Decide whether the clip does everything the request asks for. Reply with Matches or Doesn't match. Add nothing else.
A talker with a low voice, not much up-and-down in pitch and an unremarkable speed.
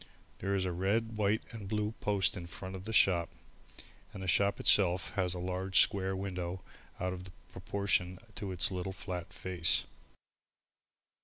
Matches